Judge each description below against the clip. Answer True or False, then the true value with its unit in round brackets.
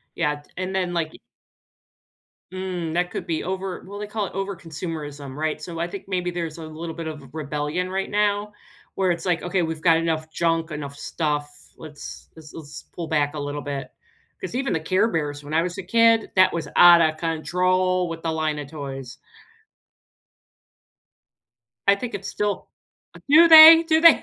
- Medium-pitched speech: True (170 Hz)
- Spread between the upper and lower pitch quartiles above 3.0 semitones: True (3.4 semitones)